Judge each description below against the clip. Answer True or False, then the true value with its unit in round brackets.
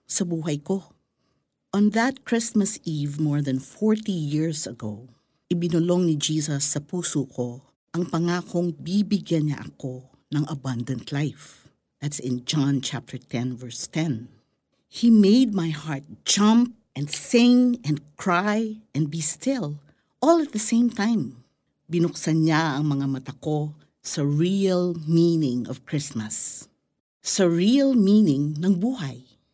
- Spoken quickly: False (135 wpm)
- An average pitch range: False (5.8 semitones)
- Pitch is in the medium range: True (160 Hz)